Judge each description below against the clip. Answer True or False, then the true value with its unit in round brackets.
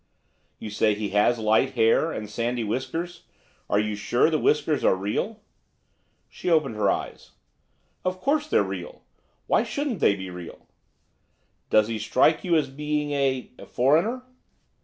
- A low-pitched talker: True (130 Hz)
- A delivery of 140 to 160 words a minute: True (150 wpm)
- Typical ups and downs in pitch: False (7.3 semitones)